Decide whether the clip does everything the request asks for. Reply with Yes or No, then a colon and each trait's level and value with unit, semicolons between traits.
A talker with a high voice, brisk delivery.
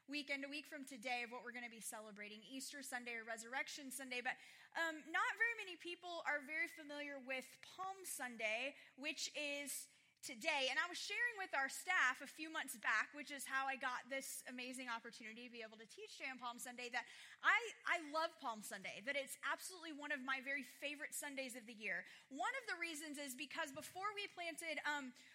Yes: very high, 280 Hz; fast, 210 wpm